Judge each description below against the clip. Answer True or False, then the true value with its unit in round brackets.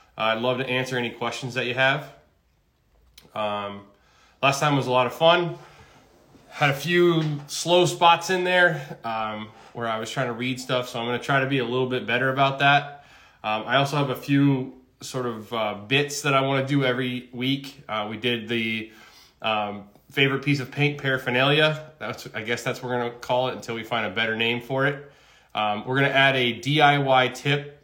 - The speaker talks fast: True (215 wpm)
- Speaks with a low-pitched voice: True (130 Hz)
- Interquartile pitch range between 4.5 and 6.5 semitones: False (3.1 semitones)